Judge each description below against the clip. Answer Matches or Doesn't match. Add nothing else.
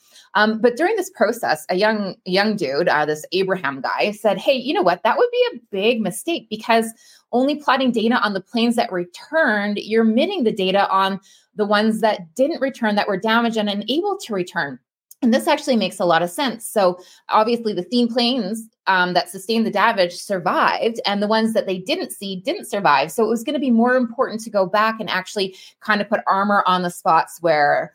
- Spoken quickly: Matches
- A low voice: Doesn't match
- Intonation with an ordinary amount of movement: Matches